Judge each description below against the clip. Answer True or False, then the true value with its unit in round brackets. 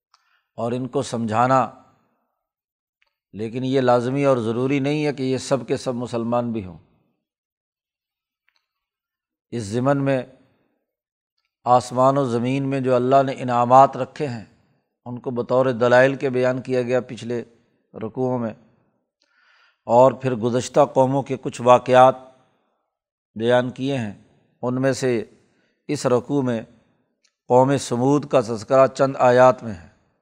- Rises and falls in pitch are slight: True (1.8 semitones)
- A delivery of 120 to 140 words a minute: True (135 wpm)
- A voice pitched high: False (125 Hz)